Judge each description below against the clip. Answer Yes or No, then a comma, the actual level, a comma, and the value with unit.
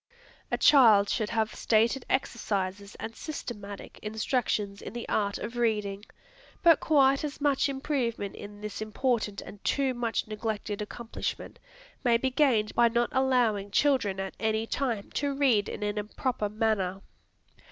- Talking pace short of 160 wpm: Yes, average, 145 wpm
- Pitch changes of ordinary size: Yes, average, 3.9 semitones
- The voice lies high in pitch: Yes, high, 225 Hz